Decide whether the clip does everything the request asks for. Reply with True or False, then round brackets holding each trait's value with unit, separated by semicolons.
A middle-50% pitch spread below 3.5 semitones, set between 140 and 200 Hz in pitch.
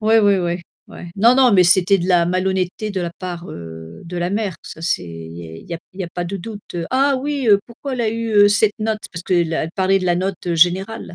False (3.8 semitones; 185 Hz)